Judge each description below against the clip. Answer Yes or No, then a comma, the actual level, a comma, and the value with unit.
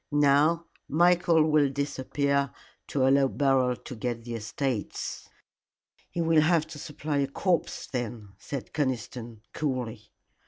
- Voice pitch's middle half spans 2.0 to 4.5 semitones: Yes, average, 3.7 semitones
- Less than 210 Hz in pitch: Yes, medium, 140 Hz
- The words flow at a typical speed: No, slow, 125 wpm